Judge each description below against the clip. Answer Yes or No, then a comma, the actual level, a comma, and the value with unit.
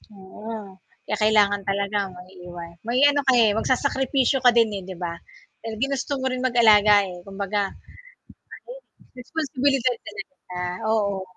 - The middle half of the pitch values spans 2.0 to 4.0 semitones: No, average, 4.6 semitones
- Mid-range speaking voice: No, high, 215 Hz